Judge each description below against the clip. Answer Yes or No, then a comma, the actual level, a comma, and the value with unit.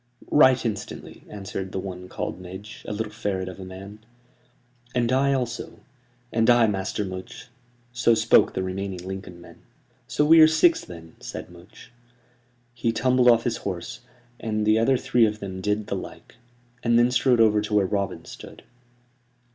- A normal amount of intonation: Yes, average, 4.0 semitones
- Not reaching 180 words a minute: Yes, average, 170 wpm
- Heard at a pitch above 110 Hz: No, low, 105 Hz